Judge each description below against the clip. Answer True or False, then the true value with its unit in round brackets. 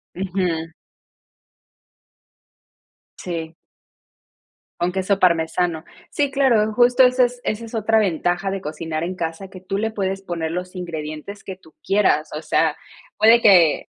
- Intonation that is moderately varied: True (4.4 semitones)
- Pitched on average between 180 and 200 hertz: True (185 Hz)